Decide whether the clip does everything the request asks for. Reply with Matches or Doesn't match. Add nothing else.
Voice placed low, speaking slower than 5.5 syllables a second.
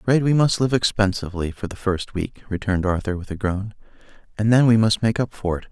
Doesn't match